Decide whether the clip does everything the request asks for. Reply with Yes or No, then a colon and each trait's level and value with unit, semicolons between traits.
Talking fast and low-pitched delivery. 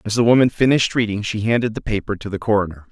Yes: fast, 245 wpm; low, 110 Hz